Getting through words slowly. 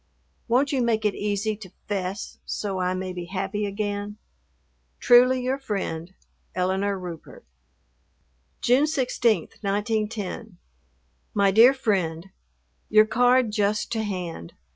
Yes: slow, 120 wpm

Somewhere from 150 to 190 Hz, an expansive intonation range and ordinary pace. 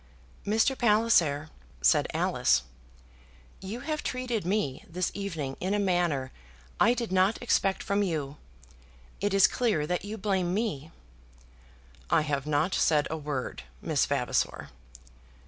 No: medium, 185 Hz; wide, 5.9 semitones; slow, 130 wpm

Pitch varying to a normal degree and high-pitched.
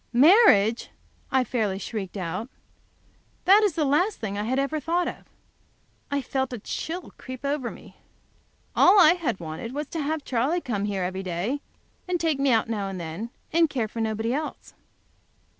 No: wide, 6.9 semitones; very high, 255 Hz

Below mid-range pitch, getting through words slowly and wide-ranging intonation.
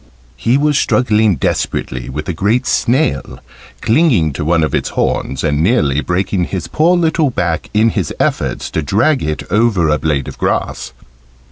No: very low, 95 Hz; average, 165 wpm; wide, 8.0 semitones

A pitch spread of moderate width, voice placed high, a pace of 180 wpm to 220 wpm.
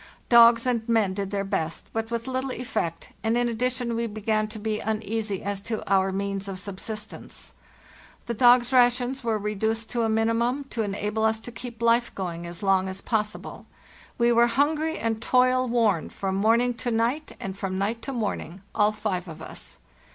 Yes: average, 3.1 semitones; high, 225 Hz; average, 190 wpm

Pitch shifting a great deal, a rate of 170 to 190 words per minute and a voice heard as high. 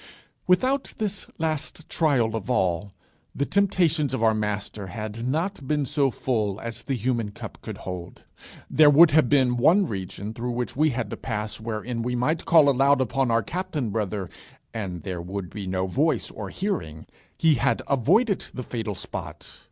No: wide, 6.3 semitones; average, 175 wpm; low, 125 Hz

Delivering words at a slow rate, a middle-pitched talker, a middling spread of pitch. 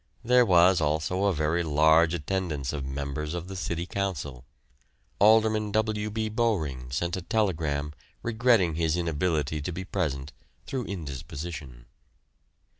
No: slow, 130 wpm; very low, 85 Hz; average, 4.9 semitones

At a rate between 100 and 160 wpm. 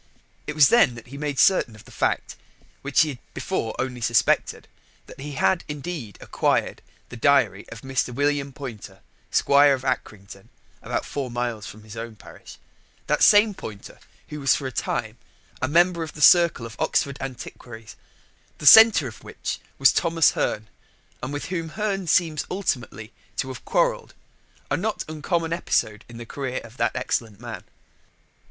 No: average, 170 wpm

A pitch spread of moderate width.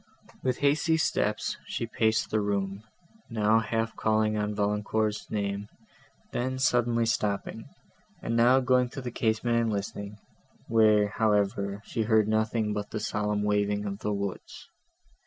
No: narrow, 2.0 semitones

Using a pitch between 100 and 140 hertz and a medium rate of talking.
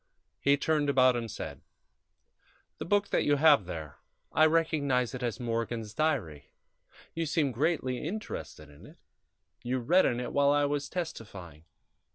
Yes: low, 135 Hz; average, 155 wpm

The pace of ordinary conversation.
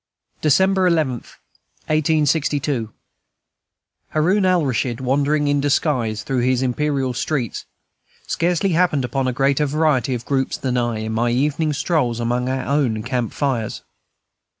No: slow, 125 wpm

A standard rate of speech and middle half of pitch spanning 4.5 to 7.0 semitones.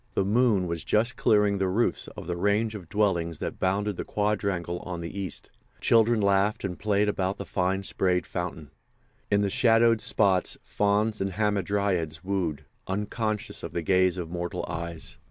No: average, 170 wpm; average, 2.8 semitones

